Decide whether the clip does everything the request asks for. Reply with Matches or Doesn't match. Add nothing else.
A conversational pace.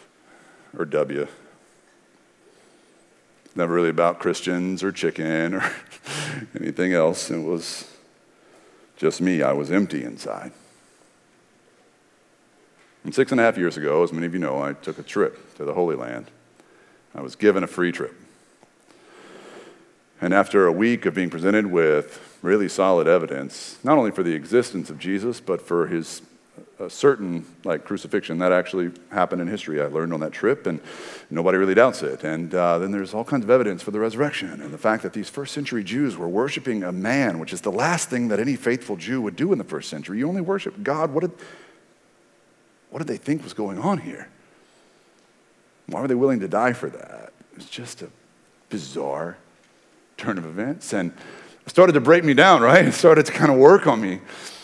Matches